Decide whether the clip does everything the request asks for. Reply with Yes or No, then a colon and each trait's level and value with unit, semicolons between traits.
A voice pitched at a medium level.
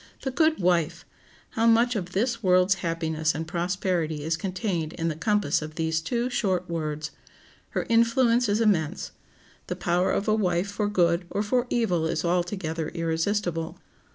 Yes: medium, 180 Hz